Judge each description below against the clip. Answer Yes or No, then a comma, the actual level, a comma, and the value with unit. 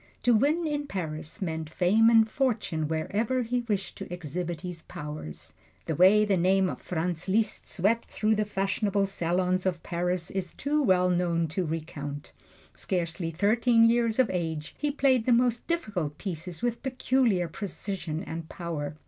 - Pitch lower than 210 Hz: Yes, medium, 185 Hz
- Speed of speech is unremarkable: Yes, average, 160 wpm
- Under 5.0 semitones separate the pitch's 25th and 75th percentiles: No, average, 5.3 semitones